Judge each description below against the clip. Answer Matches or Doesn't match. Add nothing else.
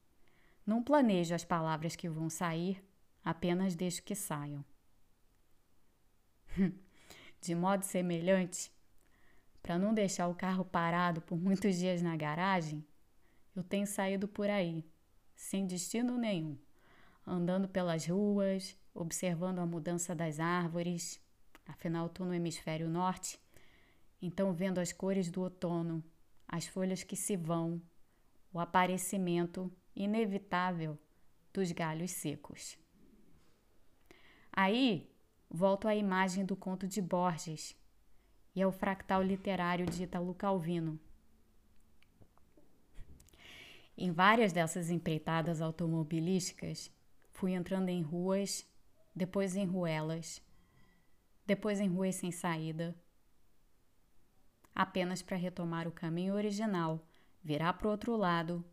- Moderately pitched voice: Matches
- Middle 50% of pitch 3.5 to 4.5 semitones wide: Doesn't match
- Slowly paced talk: Matches